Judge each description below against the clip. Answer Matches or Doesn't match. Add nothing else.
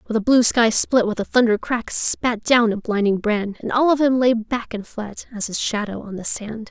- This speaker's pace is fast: Matches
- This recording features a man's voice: Doesn't match